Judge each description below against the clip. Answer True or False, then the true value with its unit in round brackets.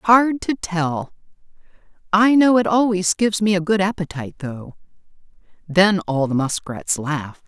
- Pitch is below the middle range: False (185 Hz)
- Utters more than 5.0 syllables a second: False (4.6 syllables/s)